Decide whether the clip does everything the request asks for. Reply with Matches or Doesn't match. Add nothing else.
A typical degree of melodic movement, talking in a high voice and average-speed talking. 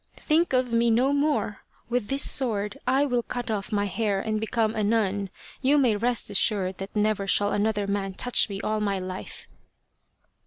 Matches